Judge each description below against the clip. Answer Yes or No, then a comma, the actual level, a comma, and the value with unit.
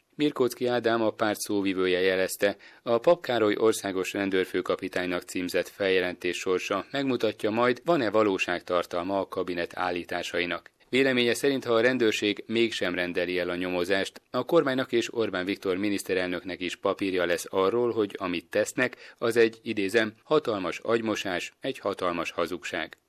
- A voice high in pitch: No, low, 105 Hz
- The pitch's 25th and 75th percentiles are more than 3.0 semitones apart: Yes, average, 4.5 semitones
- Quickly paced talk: No, average, 135 wpm